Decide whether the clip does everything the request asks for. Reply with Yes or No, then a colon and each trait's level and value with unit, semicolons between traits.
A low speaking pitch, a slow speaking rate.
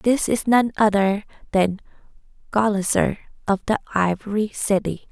No: high, 205 Hz; slow, 115 wpm